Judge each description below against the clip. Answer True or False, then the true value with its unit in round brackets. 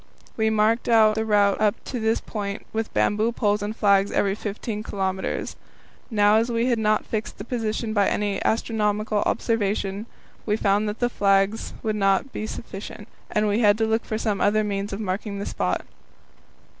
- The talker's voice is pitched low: False (210 Hz)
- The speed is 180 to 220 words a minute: True (185 wpm)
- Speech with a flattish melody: True (1.6 semitones)